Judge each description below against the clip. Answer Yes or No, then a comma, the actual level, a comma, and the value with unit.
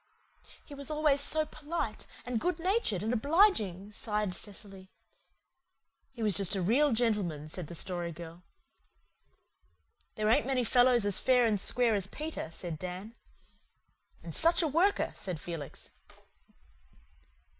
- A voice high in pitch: Yes, high, 220 Hz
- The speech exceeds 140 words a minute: No, slow, 135 wpm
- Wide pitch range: Yes, wide, 7.2 semitones